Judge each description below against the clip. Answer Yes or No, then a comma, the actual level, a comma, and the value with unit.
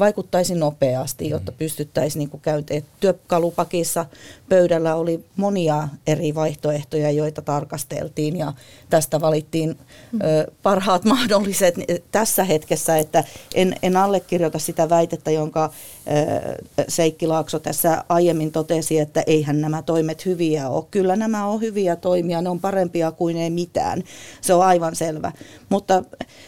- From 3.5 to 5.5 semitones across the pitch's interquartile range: No, average, 2.7 semitones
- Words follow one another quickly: No, average, 120 wpm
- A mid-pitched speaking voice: Yes, medium, 165 Hz